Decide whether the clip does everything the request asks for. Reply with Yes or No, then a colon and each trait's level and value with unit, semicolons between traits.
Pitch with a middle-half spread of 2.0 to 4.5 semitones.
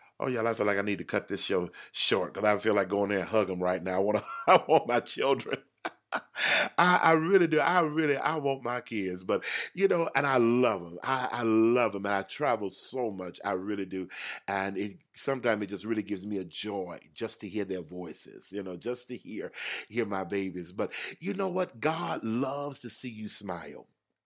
No: average, 5.3 semitones